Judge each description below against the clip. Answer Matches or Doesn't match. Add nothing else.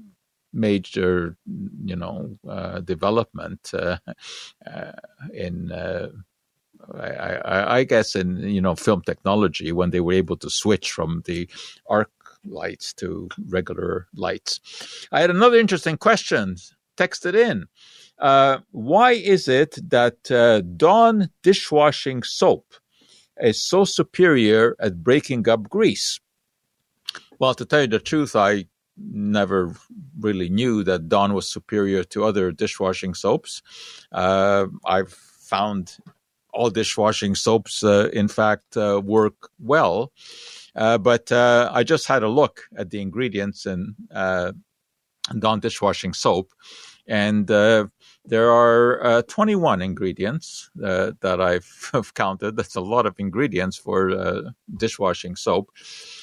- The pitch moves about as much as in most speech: Doesn't match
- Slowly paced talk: Matches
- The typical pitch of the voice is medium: Doesn't match